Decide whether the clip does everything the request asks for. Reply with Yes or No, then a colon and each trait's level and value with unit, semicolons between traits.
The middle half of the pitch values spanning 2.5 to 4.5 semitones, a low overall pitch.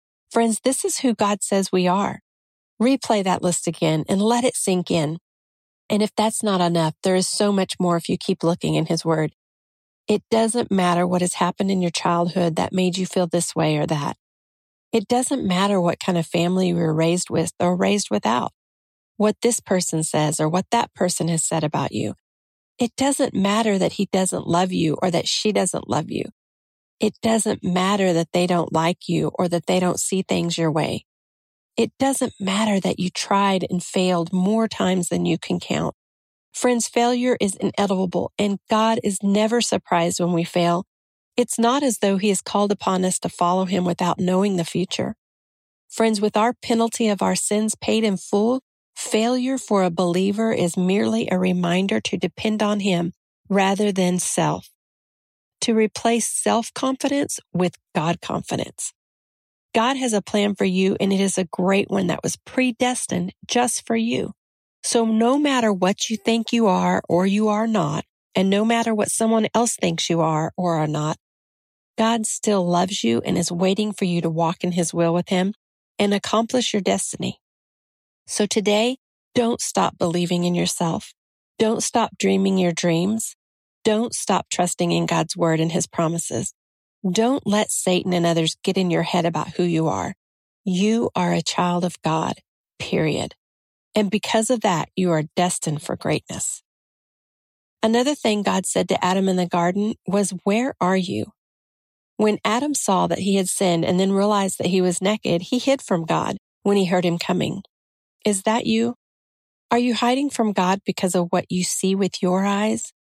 No: average, 3.9 semitones; high, 190 Hz